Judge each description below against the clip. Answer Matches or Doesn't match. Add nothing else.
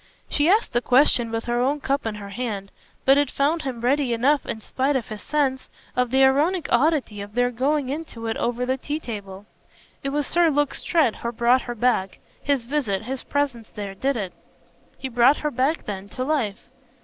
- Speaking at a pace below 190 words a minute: Doesn't match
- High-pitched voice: Matches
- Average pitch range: Matches